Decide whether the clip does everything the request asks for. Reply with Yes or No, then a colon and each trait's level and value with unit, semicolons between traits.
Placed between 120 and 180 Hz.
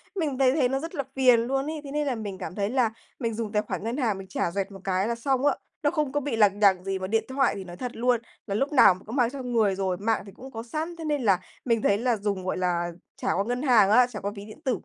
No: high, 230 Hz